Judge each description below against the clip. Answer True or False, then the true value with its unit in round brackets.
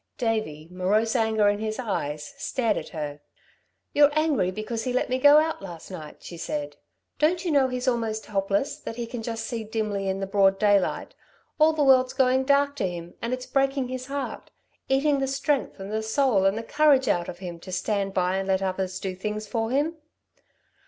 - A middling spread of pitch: False (5.7 semitones)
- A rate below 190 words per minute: False (205 wpm)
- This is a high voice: True (225 Hz)